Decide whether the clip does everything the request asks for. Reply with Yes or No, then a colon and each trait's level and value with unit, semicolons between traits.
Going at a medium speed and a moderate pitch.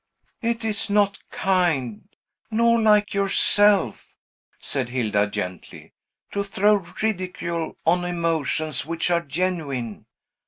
No: slow, 105 wpm; medium, 175 Hz